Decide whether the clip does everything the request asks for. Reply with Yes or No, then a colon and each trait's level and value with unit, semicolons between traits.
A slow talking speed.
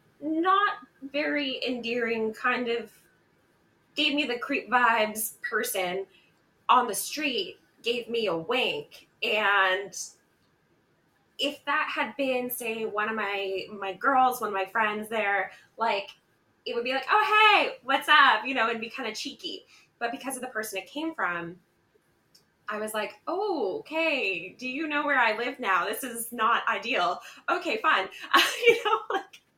No: average, 160 wpm